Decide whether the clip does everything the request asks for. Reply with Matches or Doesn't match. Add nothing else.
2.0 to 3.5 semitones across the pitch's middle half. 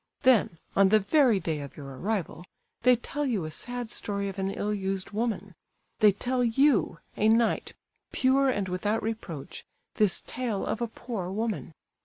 Doesn't match